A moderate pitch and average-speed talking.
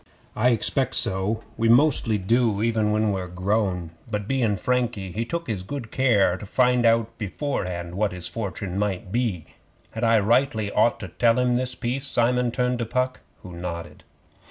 No: low, 115 Hz; average, 170 wpm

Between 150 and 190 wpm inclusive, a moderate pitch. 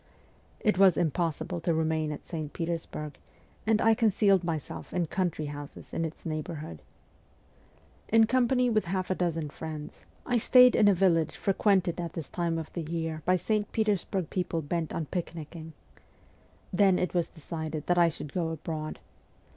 Yes: average, 165 wpm; medium, 170 Hz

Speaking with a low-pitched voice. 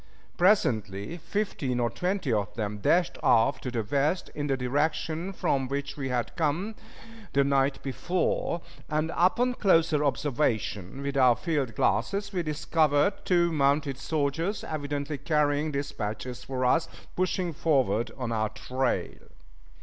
No: medium, 145 Hz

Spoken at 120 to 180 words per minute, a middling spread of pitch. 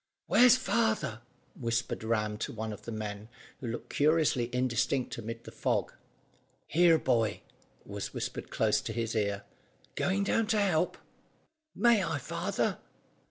No: average, 140 wpm; wide, 8.0 semitones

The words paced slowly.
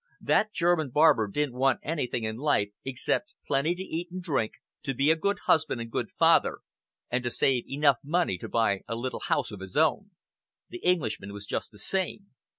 No: average, 195 wpm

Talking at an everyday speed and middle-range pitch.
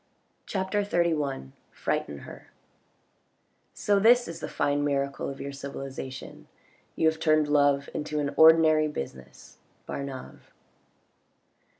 No: slow, 120 wpm; medium, 145 Hz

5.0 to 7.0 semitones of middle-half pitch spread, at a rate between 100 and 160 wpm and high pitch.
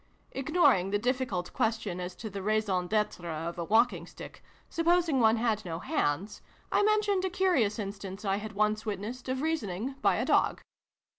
No: average, 5.3 semitones; average, 170 wpm; high, 215 Hz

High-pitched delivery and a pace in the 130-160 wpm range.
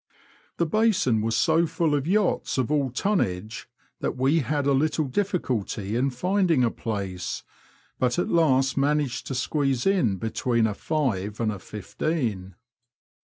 No: low, 135 Hz; average, 150 wpm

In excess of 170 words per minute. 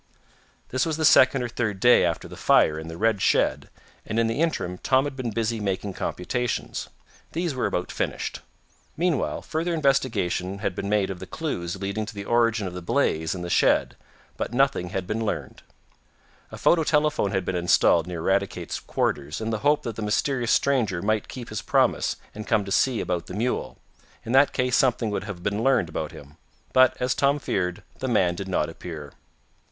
Yes: average, 195 wpm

